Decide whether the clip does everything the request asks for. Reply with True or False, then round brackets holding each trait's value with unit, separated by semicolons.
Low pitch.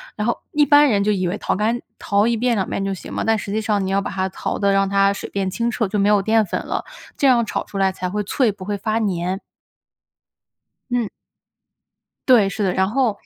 False (205 Hz)